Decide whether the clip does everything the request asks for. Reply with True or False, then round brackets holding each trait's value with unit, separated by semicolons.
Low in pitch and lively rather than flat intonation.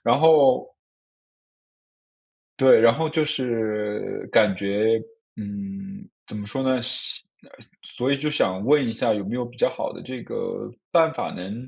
True (130 Hz; 6.0 semitones)